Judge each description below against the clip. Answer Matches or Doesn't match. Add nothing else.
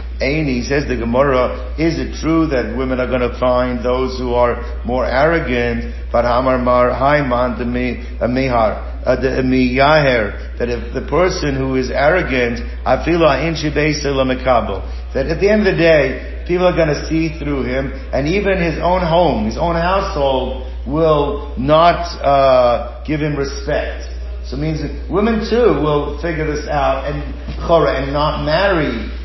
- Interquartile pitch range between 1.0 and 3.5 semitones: Doesn't match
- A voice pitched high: Doesn't match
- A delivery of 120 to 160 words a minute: Matches